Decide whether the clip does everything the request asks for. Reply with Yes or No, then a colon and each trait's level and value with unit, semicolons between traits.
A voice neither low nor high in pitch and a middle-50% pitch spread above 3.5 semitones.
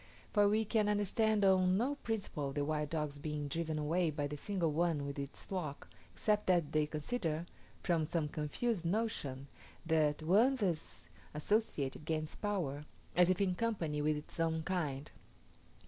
Yes: medium, 165 Hz; average, 5.1 semitones